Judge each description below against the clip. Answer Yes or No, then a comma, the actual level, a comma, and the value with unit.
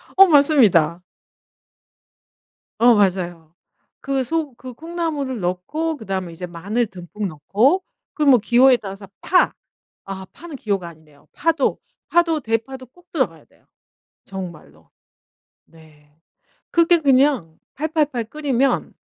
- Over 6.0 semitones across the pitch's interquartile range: Yes, wide, 8.8 semitones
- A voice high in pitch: Yes, high, 235 Hz